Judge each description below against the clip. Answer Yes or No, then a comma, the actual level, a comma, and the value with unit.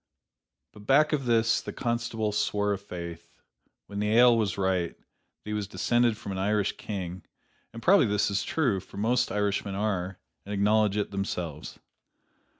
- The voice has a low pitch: Yes, low, 105 Hz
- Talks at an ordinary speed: Yes, average, 165 wpm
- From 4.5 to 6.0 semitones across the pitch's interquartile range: No, average, 2.9 semitones